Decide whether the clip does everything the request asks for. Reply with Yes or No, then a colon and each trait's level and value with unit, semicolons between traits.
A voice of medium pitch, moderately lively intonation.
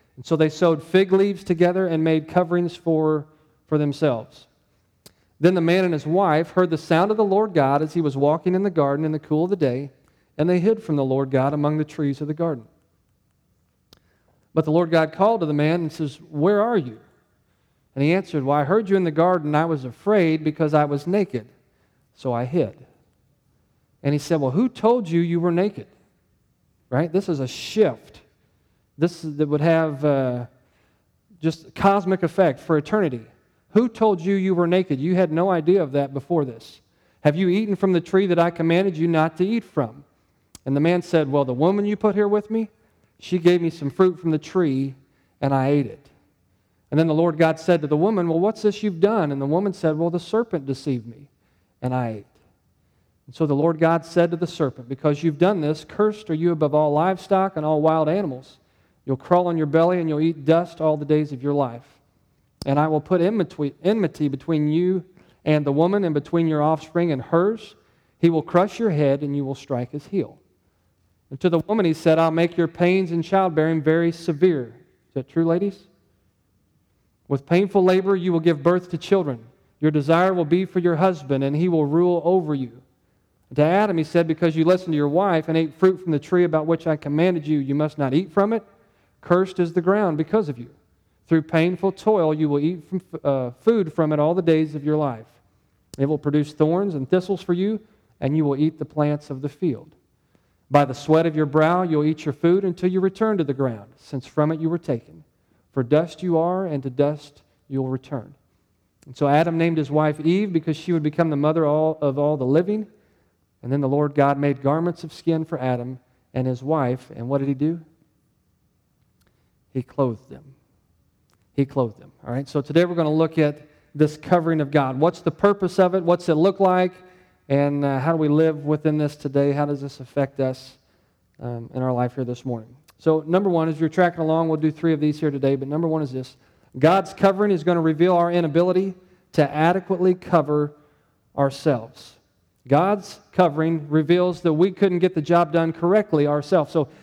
Yes: medium, 155 Hz; average, 4.0 semitones